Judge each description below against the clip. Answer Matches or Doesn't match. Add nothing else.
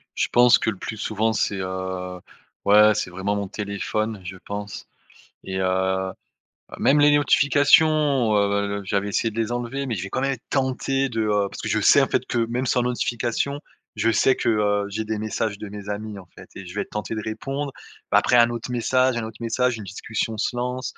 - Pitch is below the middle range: Matches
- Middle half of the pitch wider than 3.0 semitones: Matches